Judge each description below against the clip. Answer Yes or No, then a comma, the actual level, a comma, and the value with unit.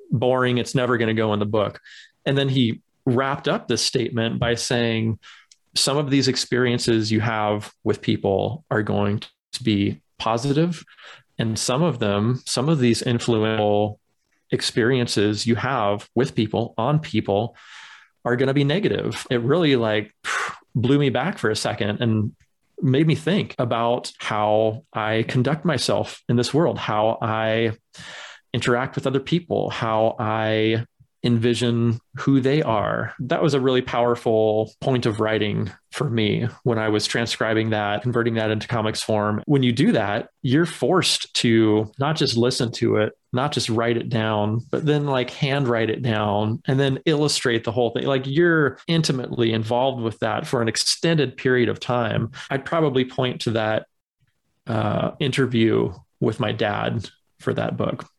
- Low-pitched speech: Yes, low, 120 Hz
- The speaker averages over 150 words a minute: Yes, average, 165 wpm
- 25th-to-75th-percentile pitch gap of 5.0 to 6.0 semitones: No, average, 3.6 semitones